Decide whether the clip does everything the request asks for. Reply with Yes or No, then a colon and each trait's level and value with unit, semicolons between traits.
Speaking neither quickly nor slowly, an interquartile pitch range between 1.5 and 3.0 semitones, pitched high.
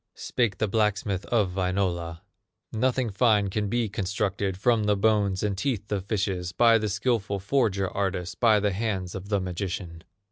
No: average, 165 wpm; narrow, 2.4 semitones; low, 100 Hz